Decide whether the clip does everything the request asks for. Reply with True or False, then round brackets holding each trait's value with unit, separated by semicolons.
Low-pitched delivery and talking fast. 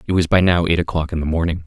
True (85 Hz; 325 wpm)